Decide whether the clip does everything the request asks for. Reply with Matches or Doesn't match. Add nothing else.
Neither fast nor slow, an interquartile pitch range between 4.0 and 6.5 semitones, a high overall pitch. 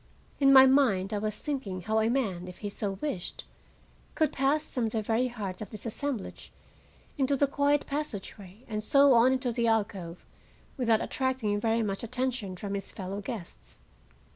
Matches